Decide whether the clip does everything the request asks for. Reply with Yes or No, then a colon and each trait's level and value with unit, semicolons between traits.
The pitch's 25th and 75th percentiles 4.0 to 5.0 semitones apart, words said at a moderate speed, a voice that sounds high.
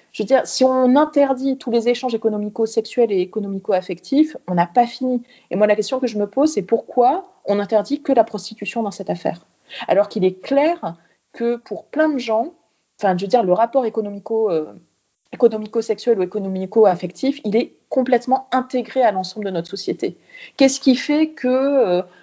Yes: average, 4.4 semitones; average, 185 wpm; high, 230 Hz